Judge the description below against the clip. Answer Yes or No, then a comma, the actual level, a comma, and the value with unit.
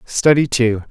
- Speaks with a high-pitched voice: No, low, 125 Hz